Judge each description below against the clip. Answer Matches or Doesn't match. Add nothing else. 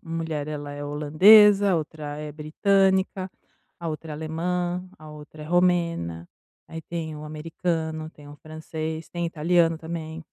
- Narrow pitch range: Matches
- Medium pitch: Matches